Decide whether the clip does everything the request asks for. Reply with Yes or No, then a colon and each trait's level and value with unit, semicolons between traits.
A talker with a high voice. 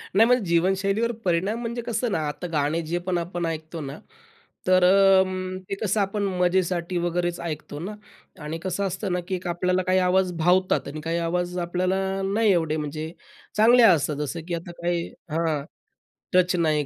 No: medium, 180 Hz